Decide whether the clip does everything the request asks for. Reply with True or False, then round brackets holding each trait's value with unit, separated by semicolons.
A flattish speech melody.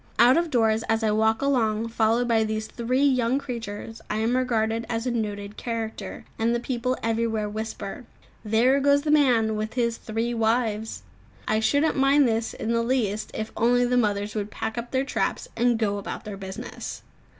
True (2.1 semitones)